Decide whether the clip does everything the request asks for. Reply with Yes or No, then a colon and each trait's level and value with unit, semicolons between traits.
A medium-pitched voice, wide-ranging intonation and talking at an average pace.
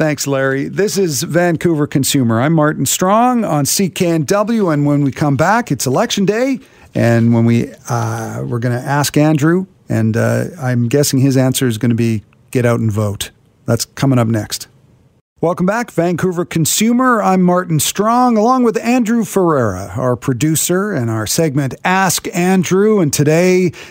Yes: medium, 150 Hz; wide, 6.8 semitones; average, 165 wpm